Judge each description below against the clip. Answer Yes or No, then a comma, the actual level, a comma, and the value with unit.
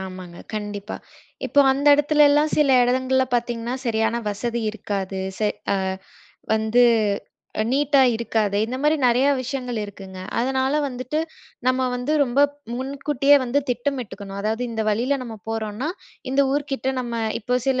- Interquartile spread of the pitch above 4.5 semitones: No, average, 3.7 semitones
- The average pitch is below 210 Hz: No, high, 245 Hz